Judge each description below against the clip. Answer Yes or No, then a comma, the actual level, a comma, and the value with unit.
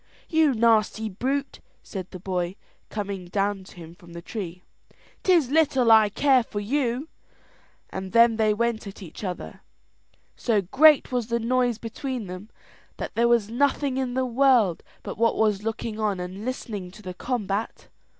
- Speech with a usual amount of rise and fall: Yes, average, 4.3 semitones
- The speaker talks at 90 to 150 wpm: No, average, 165 wpm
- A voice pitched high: Yes, high, 220 Hz